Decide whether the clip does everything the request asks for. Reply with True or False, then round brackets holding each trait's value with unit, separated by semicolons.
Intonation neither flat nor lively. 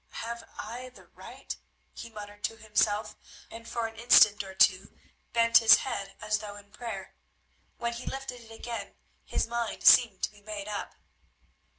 False (2.2 semitones)